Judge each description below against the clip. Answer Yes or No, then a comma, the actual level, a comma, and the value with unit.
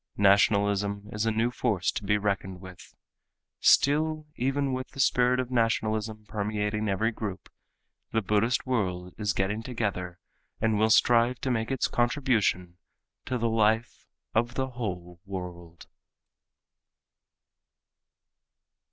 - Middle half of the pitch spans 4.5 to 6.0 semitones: No, average, 3.4 semitones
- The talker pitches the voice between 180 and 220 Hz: No, low, 110 Hz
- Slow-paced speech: Yes, slow, 125 wpm